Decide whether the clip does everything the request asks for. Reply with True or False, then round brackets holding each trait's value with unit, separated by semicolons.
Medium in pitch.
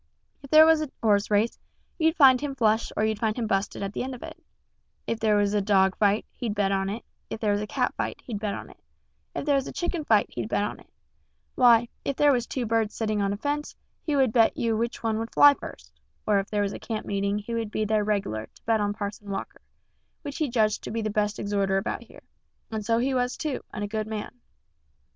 False (220 Hz)